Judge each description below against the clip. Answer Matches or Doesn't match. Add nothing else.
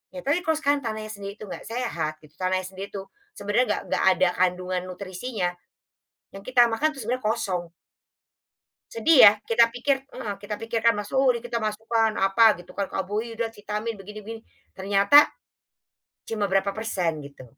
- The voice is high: Matches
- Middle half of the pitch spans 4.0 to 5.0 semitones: Doesn't match